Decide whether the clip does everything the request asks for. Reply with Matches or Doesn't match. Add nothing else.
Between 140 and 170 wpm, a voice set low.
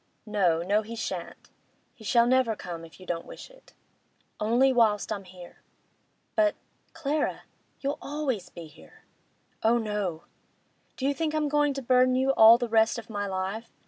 Doesn't match